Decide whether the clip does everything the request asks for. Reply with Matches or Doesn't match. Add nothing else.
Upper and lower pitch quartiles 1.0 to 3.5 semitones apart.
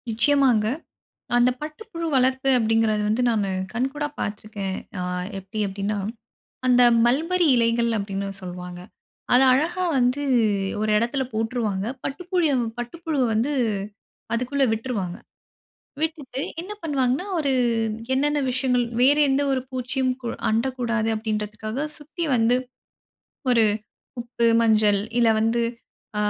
Doesn't match